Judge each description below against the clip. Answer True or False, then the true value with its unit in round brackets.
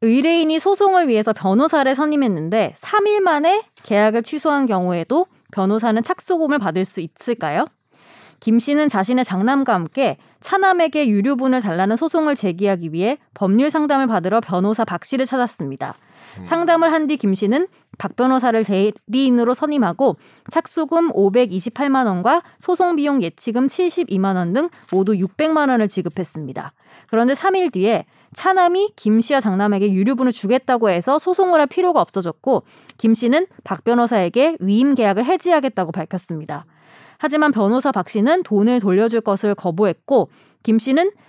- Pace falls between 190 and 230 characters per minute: False (335 characters per minute)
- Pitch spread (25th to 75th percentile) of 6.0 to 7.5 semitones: True (7.2 semitones)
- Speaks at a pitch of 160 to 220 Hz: False (245 Hz)